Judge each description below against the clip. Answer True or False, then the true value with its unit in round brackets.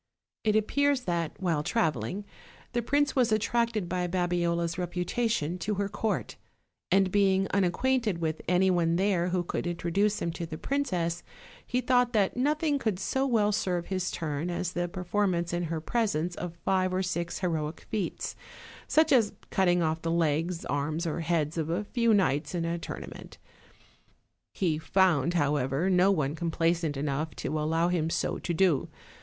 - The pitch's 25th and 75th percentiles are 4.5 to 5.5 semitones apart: False (3.7 semitones)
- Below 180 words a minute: True (165 wpm)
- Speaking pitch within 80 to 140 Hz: False (180 Hz)